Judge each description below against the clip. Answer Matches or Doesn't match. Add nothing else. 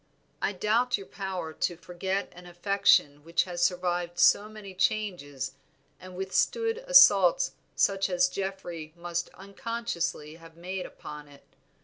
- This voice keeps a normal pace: Doesn't match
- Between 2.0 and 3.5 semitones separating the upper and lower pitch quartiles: Matches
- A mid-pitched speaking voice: Matches